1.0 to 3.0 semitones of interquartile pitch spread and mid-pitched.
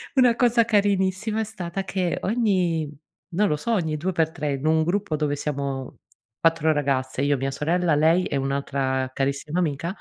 No: average, 5.1 semitones; medium, 160 Hz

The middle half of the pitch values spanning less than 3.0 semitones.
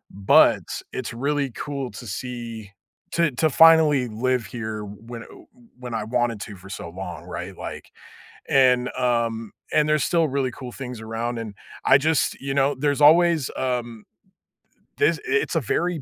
No: average, 4.0 semitones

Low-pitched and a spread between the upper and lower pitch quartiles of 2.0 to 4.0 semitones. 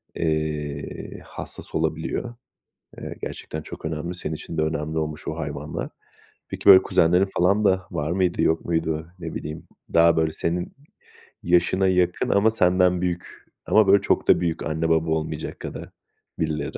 Yes: very low, 80 Hz; narrow, 2.5 semitones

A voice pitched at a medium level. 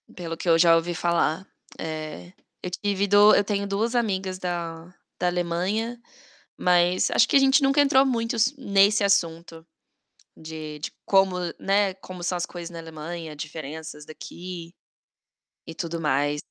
Yes: medium, 175 Hz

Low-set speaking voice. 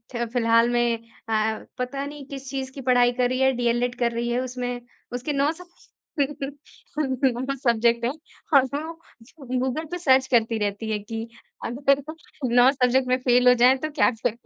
No: very high, 250 Hz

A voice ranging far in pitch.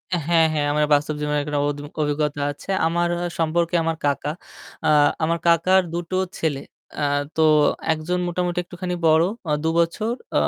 No: narrow, 2.6 semitones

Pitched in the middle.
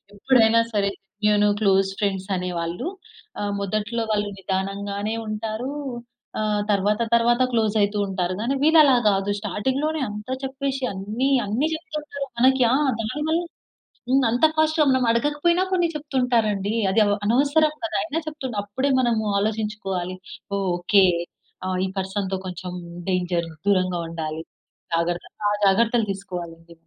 No: high, 215 Hz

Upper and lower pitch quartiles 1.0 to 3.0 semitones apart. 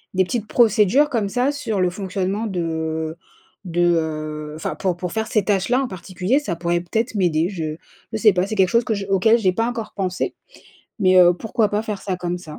No: average, 4.1 semitones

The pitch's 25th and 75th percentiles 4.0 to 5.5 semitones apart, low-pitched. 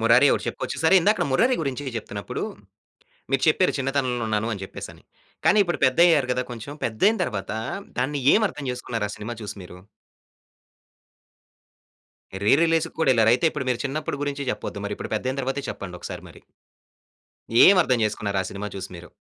Yes: average, 5.0 semitones; low, 130 Hz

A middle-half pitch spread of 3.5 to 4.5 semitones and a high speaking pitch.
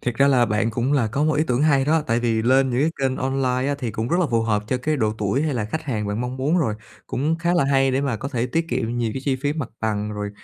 No: average, 3.8 semitones; low, 130 Hz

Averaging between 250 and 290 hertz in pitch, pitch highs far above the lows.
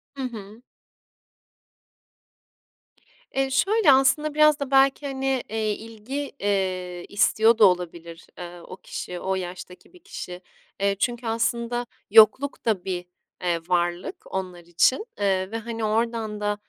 No: high, 215 Hz; wide, 6.1 semitones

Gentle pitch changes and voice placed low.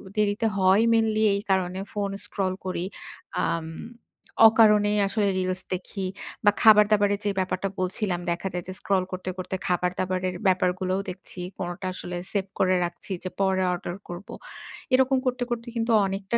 No: narrow, 2.2 semitones; high, 190 Hz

